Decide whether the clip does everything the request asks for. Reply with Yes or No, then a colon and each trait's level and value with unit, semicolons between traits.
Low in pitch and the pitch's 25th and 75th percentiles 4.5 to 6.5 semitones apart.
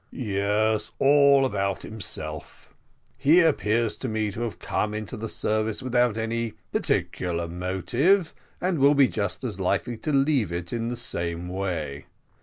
Yes: low, 110 Hz; wide, 5.4 semitones